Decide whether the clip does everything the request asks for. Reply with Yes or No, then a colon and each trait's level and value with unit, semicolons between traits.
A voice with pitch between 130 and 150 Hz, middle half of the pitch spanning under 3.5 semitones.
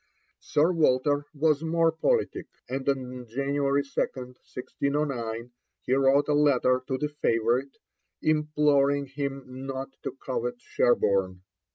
Yes: medium, 140 Hz; narrow, 2.4 semitones